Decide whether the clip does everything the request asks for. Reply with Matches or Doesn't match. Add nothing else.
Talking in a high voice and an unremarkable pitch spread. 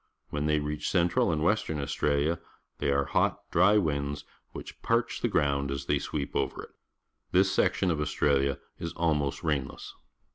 Doesn't match